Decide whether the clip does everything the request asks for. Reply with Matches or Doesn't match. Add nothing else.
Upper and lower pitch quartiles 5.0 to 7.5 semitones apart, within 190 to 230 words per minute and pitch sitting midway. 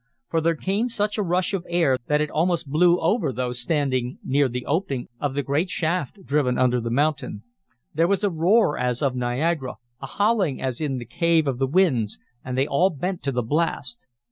Matches